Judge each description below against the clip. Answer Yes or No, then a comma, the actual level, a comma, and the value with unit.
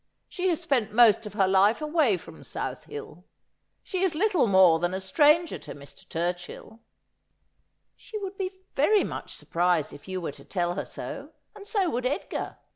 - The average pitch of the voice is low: No, high, 230 Hz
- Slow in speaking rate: No, average, 185 wpm